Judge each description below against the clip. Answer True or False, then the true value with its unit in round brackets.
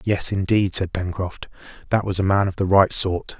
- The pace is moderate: False (210 wpm)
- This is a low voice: True (95 Hz)